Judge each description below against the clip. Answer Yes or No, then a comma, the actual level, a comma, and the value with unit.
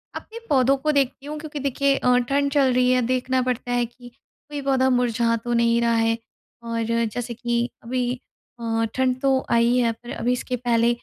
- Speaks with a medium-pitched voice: No, very high, 250 Hz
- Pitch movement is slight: Yes, narrow, 2.2 semitones